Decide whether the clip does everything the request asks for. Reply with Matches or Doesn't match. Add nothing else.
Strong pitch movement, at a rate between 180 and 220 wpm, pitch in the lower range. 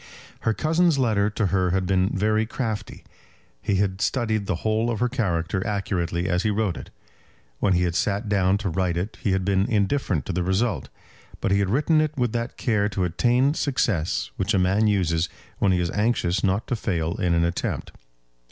Doesn't match